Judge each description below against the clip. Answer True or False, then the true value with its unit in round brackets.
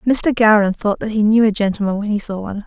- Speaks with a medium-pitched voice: False (210 Hz)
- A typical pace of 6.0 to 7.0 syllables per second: True (6.4 syllables/s)